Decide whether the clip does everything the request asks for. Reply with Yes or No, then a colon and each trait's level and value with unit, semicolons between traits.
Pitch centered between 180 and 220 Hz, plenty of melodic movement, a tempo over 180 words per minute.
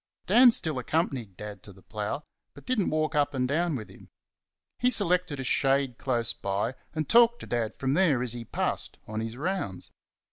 No: low, 135 Hz; wide, 6.8 semitones; average, 200 wpm